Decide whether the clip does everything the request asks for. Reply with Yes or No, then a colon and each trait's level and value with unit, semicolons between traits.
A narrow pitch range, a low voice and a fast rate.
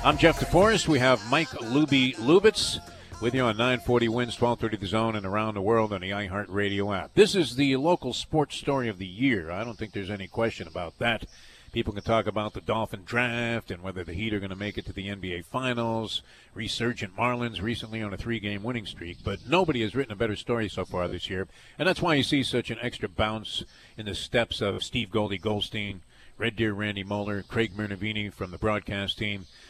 No: average, 3.3 semitones; low, 110 Hz; fast, 215 wpm